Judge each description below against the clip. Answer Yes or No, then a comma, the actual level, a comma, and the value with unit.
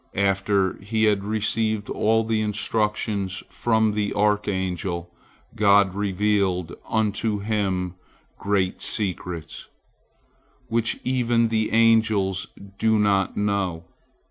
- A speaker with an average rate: No, slow, 95 wpm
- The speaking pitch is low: Yes, low, 105 Hz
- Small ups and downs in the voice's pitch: Yes, narrow, 2.2 semitones